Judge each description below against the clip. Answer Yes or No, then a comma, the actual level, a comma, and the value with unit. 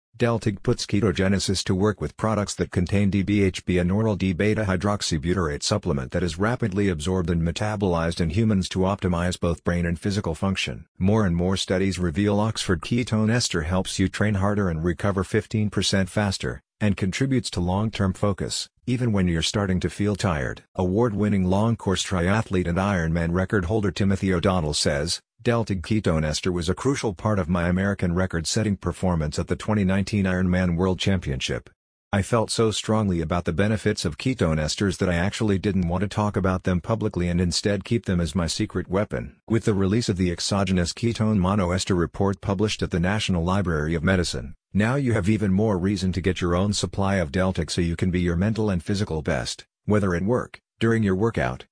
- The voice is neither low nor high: No, very low, 95 Hz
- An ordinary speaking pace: Yes, average, 185 wpm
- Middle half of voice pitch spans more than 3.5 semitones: No, average, 2.8 semitones